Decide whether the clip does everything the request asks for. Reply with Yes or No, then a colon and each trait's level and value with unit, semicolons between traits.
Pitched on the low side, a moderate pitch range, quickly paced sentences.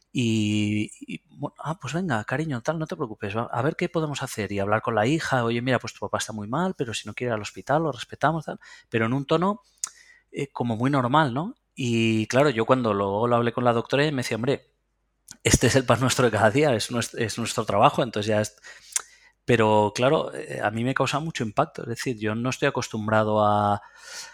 Yes: low, 120 Hz; average, 4.4 semitones; fast, 230 wpm